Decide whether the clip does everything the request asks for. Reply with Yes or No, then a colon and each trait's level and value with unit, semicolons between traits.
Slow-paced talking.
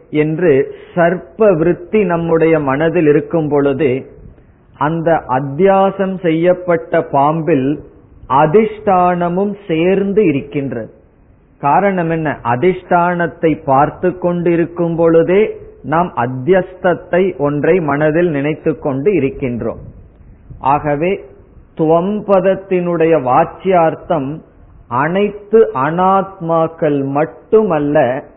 Yes: slow, 70 wpm